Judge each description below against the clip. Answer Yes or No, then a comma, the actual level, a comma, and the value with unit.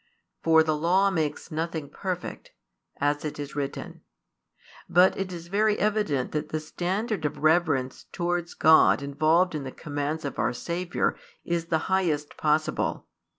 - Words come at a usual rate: Yes, average, 150 wpm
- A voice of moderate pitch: Yes, medium, 160 Hz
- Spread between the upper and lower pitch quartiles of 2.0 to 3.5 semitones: Yes, average, 3.1 semitones